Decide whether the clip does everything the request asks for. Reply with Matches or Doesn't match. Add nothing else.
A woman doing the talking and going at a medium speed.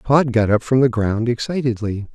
Doesn't match